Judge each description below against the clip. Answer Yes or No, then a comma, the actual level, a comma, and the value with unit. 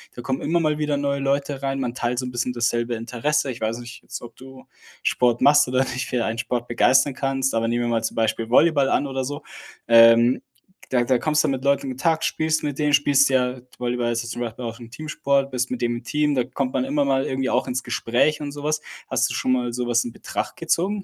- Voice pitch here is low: Yes, low, 130 Hz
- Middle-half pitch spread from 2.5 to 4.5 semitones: Yes, average, 2.8 semitones